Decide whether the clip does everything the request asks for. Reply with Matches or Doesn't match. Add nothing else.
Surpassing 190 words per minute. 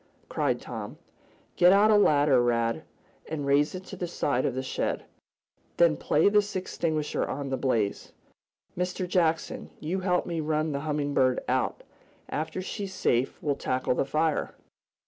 Doesn't match